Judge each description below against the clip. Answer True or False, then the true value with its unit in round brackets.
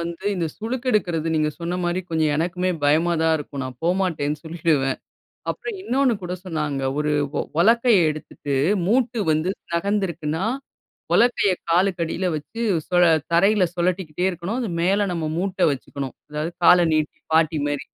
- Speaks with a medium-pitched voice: True (170 Hz)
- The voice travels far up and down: False (3.9 semitones)